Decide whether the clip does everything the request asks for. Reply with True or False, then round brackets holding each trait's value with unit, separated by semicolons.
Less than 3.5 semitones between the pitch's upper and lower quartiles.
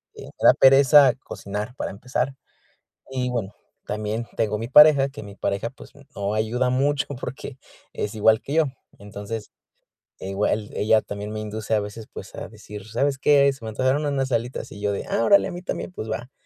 False (4.3 semitones)